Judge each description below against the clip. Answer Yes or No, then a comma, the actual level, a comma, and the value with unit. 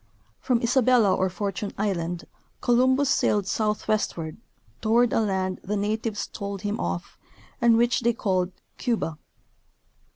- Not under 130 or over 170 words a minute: Yes, slow, 135 wpm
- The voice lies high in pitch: Yes, high, 210 Hz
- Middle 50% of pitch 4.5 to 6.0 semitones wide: No, average, 3.8 semitones